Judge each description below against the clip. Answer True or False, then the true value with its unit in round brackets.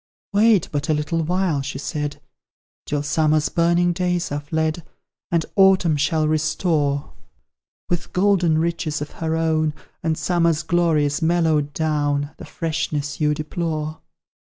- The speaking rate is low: True (130 wpm)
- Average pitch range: False (2.3 semitones)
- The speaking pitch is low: False (160 Hz)